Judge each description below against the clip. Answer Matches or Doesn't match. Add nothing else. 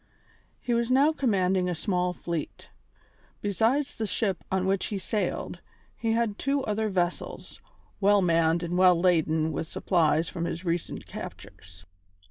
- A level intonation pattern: Doesn't match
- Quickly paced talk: Doesn't match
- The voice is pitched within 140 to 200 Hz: Matches